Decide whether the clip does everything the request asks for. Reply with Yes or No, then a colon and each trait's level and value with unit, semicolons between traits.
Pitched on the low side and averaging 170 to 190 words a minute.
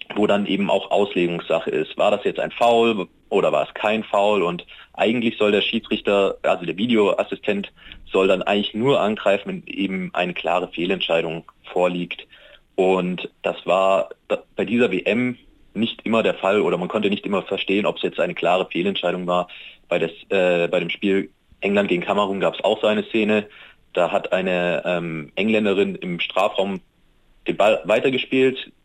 Yes: low, 100 Hz; average, 175 wpm